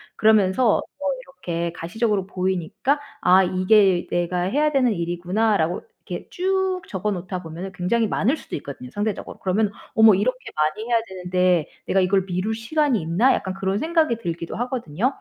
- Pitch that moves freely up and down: No, average, 4.6 semitones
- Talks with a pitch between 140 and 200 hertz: Yes, high, 195 Hz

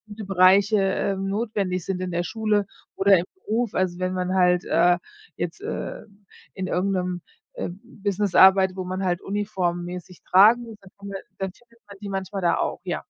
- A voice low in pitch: No, high, 190 Hz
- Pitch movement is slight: Yes, narrow, 1.8 semitones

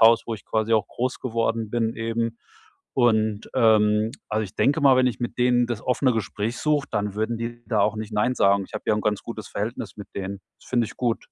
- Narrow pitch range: Yes, narrow, 2.1 semitones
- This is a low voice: Yes, low, 115 Hz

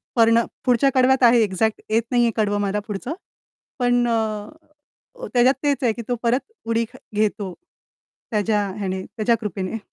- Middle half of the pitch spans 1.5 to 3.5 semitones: Yes, average, 2.7 semitones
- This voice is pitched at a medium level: No, high, 225 Hz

